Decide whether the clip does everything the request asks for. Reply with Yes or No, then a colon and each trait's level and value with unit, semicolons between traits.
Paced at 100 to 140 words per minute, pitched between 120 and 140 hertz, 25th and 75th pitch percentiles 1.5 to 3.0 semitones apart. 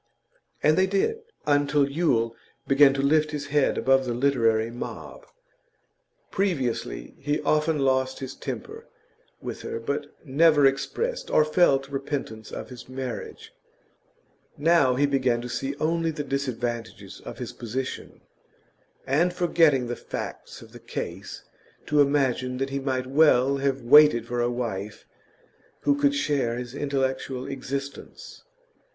Yes: slow, 135 wpm; low, 135 Hz; average, 2.7 semitones